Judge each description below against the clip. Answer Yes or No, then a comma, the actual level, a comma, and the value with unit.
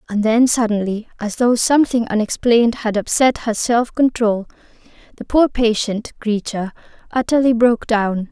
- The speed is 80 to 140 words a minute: Yes, slow, 135 wpm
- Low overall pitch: No, high, 230 Hz